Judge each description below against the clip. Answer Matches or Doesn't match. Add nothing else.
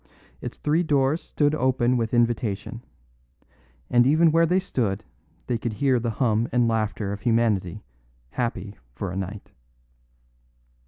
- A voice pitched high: Doesn't match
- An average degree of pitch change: Matches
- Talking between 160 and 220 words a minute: Doesn't match